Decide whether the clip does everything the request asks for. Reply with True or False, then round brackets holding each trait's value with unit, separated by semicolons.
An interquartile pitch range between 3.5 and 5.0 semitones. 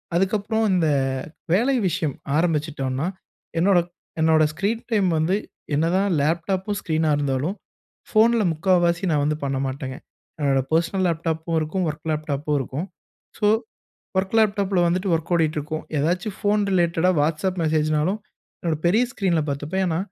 True (3.8 semitones)